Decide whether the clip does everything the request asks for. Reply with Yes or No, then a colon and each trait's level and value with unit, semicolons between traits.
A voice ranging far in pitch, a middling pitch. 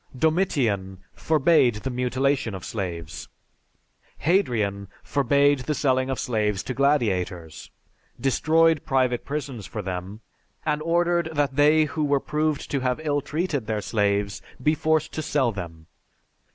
No: wide, 6.3 semitones; low, 130 Hz